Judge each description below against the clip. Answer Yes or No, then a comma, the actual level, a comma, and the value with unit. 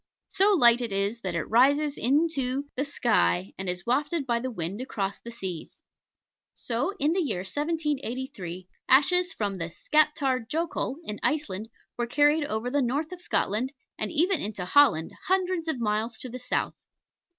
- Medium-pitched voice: No, very high, 255 Hz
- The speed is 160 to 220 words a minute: Yes, average, 165 wpm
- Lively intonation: Yes, wide, 6.2 semitones